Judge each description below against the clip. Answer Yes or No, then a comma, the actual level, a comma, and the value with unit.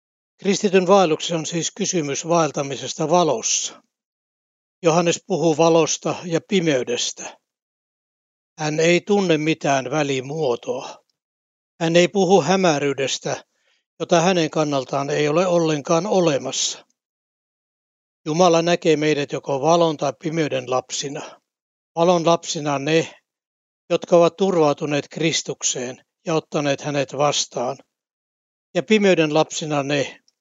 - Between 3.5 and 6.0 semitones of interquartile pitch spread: No, average, 3.0 semitones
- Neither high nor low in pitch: Yes, medium, 160 Hz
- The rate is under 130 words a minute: Yes, average, 100 wpm